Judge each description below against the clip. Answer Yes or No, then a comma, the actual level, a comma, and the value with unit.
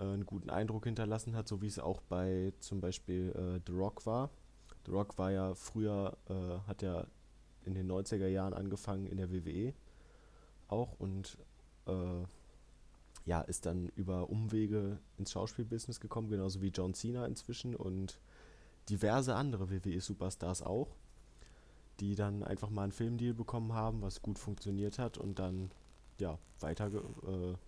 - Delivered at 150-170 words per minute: Yes, average, 155 wpm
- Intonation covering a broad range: No, average, 2.7 semitones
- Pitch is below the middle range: Yes, very low, 95 Hz